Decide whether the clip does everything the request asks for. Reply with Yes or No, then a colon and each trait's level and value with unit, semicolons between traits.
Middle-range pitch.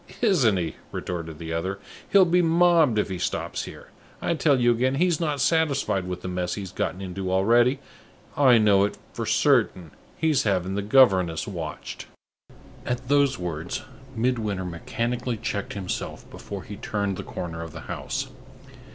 No: low, 105 Hz